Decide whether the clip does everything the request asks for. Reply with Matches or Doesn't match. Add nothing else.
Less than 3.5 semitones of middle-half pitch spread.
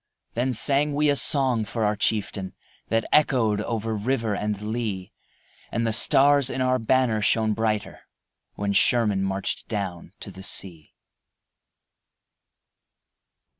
Doesn't match